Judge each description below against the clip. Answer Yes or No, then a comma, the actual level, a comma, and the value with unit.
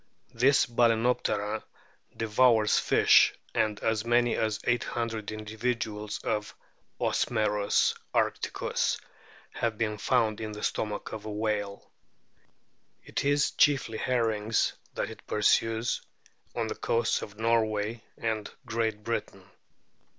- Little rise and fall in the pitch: Yes, narrow, 1.6 semitones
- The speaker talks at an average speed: No, slow, 110 wpm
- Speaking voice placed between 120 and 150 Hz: No, low, 110 Hz